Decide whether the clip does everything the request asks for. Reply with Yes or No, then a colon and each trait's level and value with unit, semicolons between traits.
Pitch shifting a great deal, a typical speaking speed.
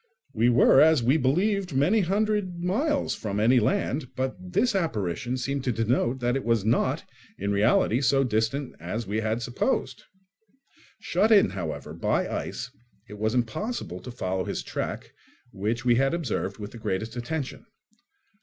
Yes: wide, 6.6 semitones; average, 160 wpm